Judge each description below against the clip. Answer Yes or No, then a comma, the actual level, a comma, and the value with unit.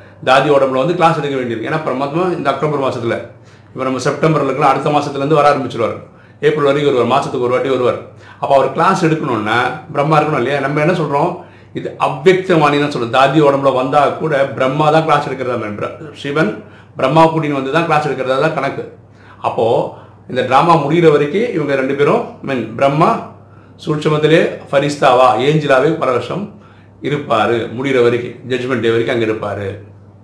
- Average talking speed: No, fast, 155 wpm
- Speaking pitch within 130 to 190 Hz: Yes, medium, 140 Hz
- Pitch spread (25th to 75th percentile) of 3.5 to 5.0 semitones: Yes, average, 3.8 semitones